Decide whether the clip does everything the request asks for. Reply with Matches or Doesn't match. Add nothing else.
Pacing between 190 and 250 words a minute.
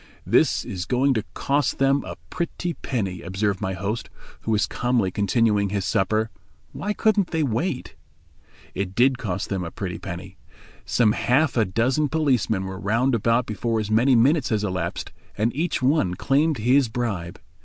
Doesn't match